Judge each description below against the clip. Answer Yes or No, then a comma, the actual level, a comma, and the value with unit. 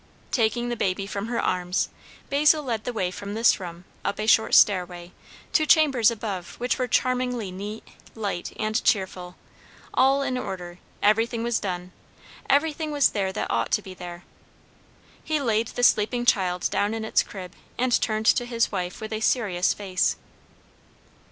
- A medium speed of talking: Yes, average, 165 wpm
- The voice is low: No, high, 215 Hz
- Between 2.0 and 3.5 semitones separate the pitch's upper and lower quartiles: No, average, 4.6 semitones